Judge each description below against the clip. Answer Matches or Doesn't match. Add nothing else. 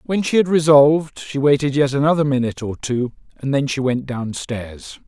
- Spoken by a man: Matches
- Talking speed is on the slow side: Doesn't match